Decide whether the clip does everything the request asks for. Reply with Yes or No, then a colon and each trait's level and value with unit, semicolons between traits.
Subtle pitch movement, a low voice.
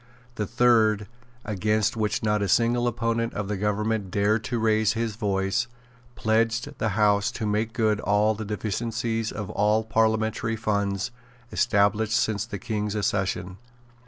Yes: narrow, 1.5 semitones; low, 110 Hz